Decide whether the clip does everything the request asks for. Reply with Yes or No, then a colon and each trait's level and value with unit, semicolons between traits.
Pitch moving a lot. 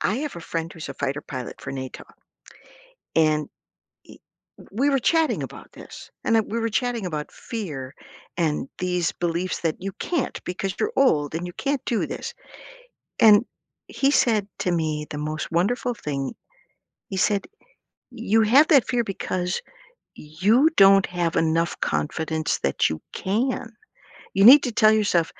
Yes: wide, 6.3 semitones